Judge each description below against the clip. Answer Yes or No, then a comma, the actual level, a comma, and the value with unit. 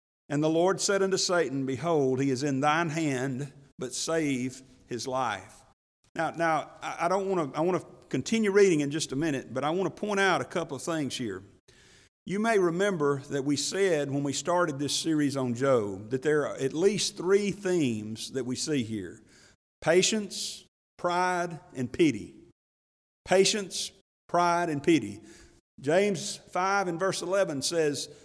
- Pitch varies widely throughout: Yes, wide, 5.9 semitones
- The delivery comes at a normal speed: Yes, average, 160 wpm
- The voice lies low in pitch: No, medium, 150 Hz